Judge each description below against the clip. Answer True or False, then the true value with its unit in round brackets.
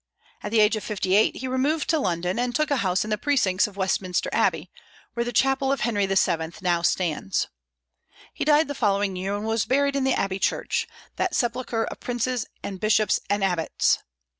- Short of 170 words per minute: False (200 wpm)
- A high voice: True (215 Hz)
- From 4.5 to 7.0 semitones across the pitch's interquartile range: True (5.3 semitones)